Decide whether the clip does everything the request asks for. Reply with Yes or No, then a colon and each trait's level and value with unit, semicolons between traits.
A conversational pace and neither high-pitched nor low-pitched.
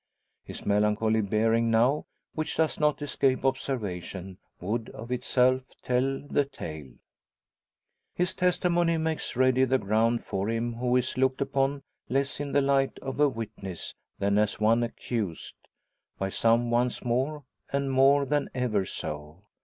No: average, 145 wpm; low, 125 Hz